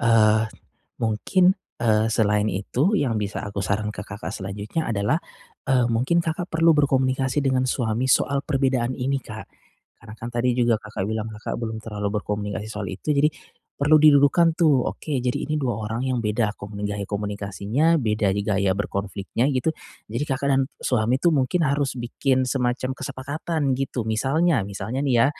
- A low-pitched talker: Yes, low, 120 Hz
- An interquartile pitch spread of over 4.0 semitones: Yes, average, 4.4 semitones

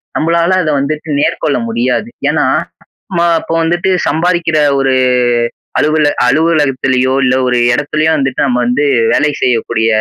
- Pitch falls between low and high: Yes, medium, 145 Hz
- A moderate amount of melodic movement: Yes, average, 4.0 semitones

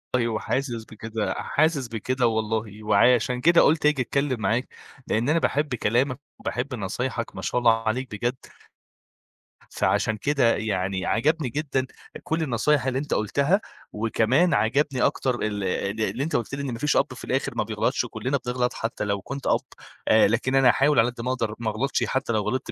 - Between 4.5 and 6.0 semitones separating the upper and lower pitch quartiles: No, average, 3.8 semitones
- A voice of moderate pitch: No, low, 125 Hz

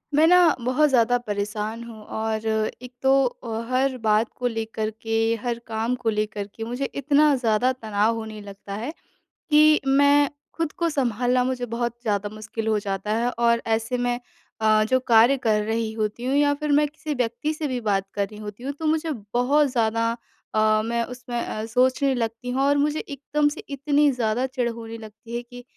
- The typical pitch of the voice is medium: No, high, 235 Hz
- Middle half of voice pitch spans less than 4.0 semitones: Yes, average, 3.6 semitones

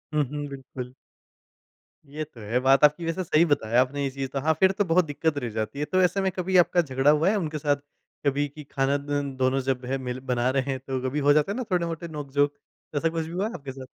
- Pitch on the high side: No, medium, 145 Hz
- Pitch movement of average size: Yes, average, 3.6 semitones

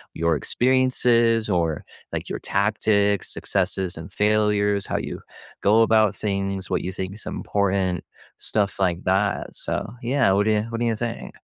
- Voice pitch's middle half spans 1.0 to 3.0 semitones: Yes, narrow, 2.5 semitones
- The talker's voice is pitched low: Yes, low, 100 Hz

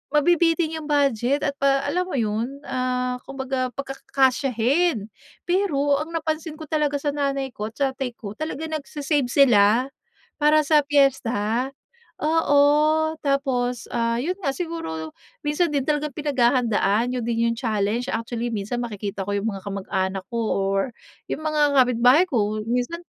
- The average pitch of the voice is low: No, very high, 270 Hz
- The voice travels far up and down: No, average, 4.2 semitones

